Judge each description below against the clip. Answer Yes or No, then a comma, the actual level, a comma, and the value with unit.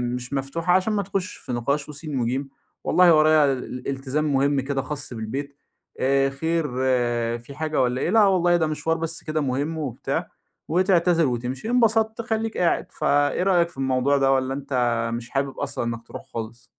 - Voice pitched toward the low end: No, medium, 145 Hz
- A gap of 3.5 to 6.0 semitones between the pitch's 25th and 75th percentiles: Yes, average, 4.2 semitones